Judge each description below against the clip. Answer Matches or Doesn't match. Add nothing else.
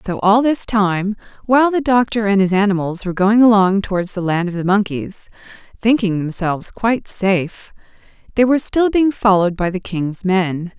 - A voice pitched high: Matches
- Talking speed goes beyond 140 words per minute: Matches